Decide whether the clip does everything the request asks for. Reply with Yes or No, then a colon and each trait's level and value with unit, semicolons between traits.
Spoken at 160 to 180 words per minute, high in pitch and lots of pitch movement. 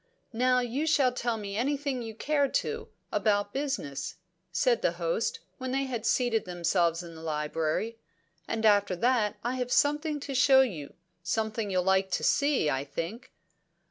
Yes: average, 165 wpm; high, 225 Hz; wide, 6.6 semitones